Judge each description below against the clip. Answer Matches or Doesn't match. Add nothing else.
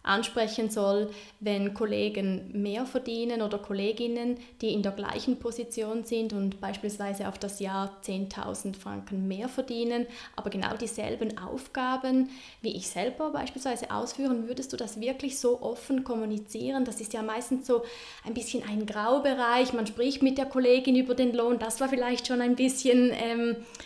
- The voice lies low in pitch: Doesn't match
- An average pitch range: Matches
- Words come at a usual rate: Matches